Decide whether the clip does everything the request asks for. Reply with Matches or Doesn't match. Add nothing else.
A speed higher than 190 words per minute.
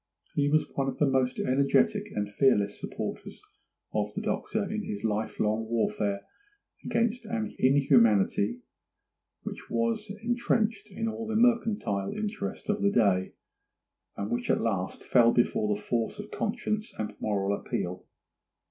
Doesn't match